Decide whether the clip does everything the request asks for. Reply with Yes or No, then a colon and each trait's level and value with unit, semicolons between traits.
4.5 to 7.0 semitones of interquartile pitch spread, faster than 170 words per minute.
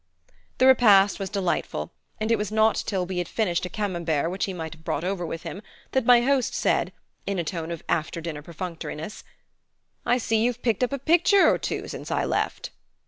Yes: average, 5.2 semitones; fast, 205 wpm